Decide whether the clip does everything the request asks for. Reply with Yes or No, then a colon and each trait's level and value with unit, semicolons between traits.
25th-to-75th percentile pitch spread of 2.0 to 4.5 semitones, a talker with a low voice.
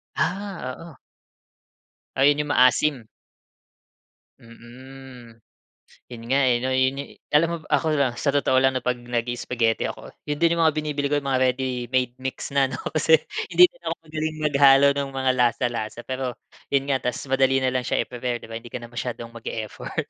Yes: average, 2.7 semitones; low, 130 Hz